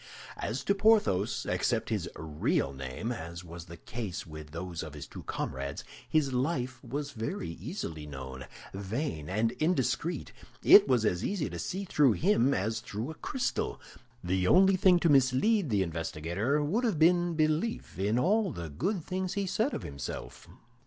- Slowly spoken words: No, average, 165 wpm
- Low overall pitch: Yes, low, 120 Hz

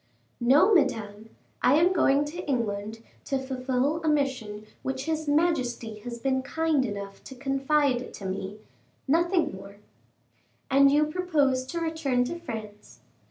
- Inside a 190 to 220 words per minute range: No, average, 140 wpm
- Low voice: No, very high, 265 Hz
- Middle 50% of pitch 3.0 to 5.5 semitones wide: Yes, average, 5.2 semitones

